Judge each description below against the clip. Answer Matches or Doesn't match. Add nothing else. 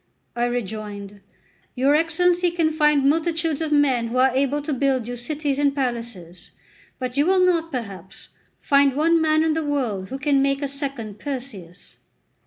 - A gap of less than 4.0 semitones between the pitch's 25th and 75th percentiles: Doesn't match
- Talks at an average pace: Matches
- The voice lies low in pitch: Doesn't match